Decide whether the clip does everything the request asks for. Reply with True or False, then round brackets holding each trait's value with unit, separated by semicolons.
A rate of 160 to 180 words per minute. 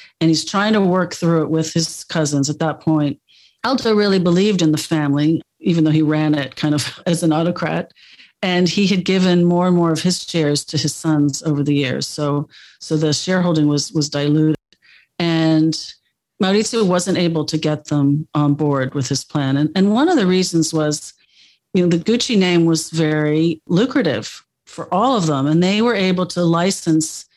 False (195 wpm)